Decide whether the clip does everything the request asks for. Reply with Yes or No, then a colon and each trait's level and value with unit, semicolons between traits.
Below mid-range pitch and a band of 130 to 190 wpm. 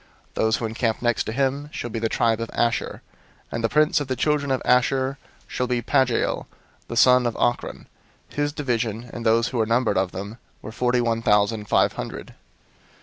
No: low, 120 Hz; fast, 205 wpm